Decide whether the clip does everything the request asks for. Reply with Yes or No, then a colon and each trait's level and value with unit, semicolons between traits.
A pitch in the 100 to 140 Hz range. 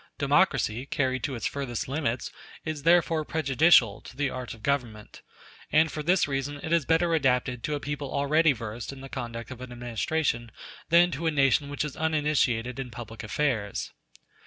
Yes: low, 135 Hz